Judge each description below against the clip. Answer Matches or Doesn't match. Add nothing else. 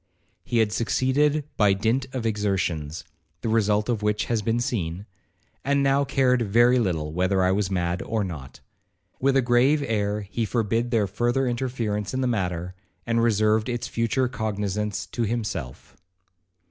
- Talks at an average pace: Matches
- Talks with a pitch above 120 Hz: Doesn't match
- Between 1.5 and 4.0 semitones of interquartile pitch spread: Matches